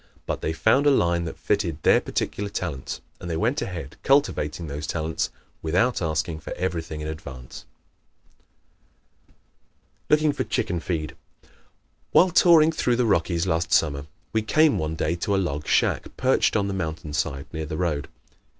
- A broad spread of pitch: Yes, wide, 5.7 semitones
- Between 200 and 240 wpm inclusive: No, average, 165 wpm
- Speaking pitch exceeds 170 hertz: No, very low, 85 Hz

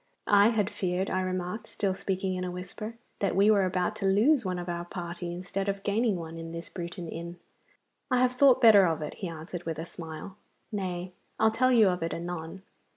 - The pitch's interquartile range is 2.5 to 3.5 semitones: Yes, average, 2.9 semitones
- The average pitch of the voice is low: No, medium, 185 Hz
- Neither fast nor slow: No, fast, 215 wpm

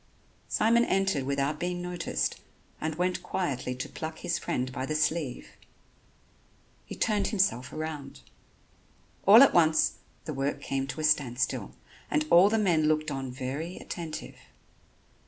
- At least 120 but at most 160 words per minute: Yes, average, 140 wpm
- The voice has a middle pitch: Yes, medium, 155 Hz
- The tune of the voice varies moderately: Yes, average, 4.5 semitones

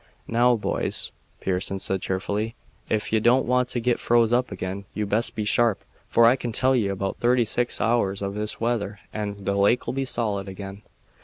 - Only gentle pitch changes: No, average, 3.3 semitones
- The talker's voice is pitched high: No, low, 110 Hz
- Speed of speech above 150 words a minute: Yes, average, 190 wpm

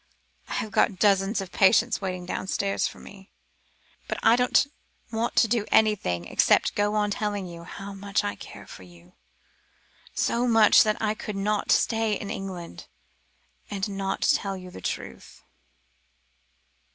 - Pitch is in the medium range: No, high, 200 Hz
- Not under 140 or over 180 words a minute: Yes, average, 150 wpm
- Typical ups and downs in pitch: No, narrow, 2.2 semitones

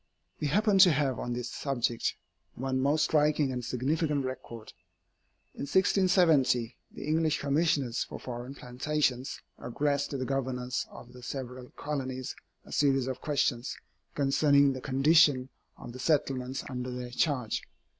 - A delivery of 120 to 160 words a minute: Yes, average, 140 wpm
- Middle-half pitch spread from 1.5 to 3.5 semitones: Yes, average, 3.0 semitones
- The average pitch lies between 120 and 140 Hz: Yes, low, 135 Hz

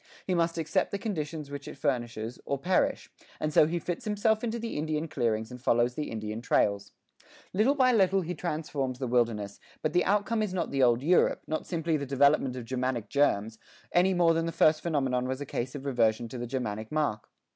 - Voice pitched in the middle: Yes, medium, 145 Hz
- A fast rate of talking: Yes, fast, 210 wpm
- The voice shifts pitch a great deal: Yes, wide, 5.9 semitones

